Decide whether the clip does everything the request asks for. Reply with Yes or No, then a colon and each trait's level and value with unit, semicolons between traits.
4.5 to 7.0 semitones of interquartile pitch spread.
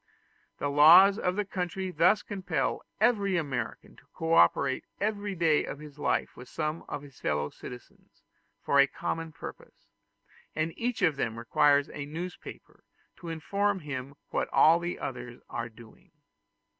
Yes: average, 4.8 semitones